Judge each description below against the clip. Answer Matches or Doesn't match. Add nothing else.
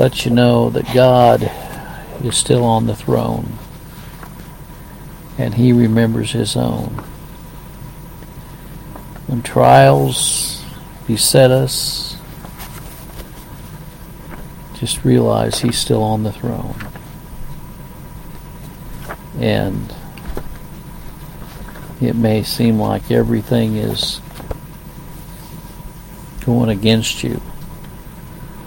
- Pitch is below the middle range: Matches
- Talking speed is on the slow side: Matches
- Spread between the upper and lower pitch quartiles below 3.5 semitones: Matches